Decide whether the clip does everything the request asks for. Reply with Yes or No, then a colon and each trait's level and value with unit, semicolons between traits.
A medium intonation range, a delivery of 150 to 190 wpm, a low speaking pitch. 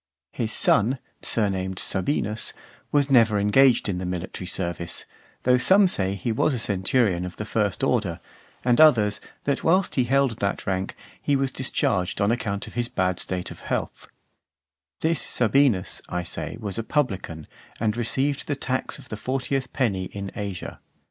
No: wide, 5.7 semitones; average, 165 wpm; low, 110 Hz